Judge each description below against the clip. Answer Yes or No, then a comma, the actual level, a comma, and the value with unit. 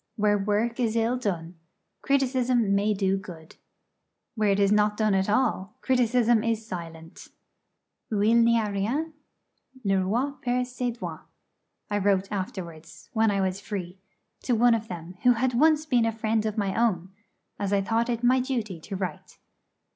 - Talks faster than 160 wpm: Yes, average, 170 wpm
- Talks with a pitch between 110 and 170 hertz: No, high, 215 Hz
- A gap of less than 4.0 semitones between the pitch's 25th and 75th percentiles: Yes, average, 3.6 semitones